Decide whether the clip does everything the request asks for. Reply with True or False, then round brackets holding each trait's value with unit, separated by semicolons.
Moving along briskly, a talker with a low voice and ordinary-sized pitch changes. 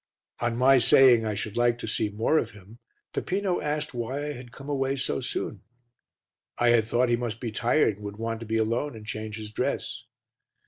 True (210 wpm; 120 Hz; 3.4 semitones)